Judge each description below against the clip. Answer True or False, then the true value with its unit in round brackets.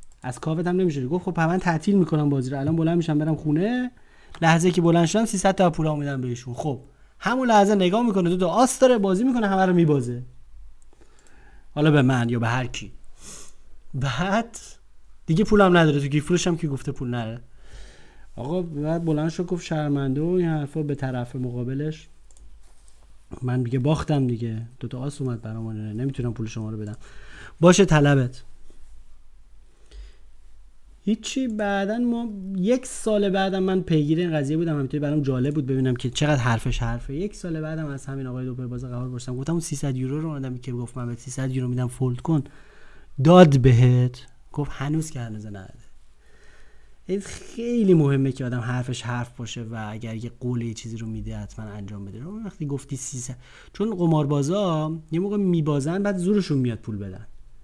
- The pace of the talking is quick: True (175 wpm)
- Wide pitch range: True (6.0 semitones)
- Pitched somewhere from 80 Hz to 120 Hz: False (140 Hz)